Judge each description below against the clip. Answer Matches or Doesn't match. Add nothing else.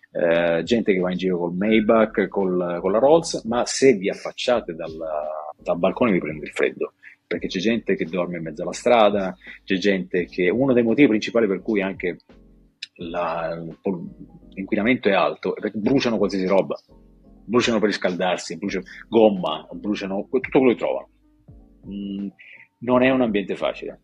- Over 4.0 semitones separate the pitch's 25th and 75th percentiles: Matches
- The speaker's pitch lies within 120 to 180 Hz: Doesn't match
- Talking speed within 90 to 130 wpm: Doesn't match